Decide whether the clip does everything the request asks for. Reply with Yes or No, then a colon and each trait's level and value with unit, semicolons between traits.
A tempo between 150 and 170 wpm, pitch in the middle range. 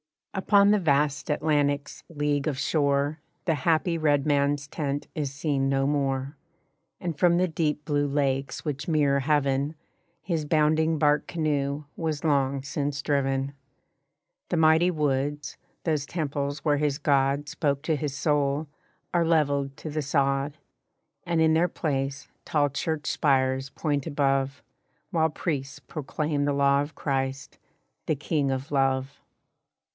No: average, 140 wpm; medium, 145 Hz